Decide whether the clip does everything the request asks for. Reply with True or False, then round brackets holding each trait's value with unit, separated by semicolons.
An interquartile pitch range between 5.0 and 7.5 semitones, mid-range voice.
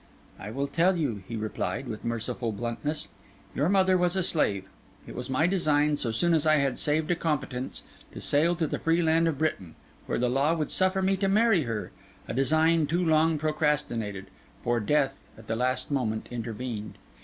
True (5.5 semitones; 145 Hz)